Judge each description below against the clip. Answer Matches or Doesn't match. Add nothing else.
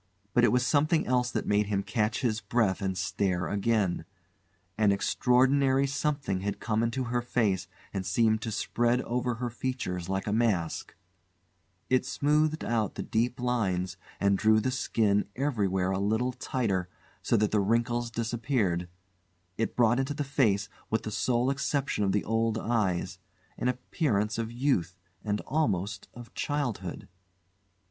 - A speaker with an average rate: Matches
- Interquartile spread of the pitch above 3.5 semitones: Matches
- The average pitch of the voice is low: Matches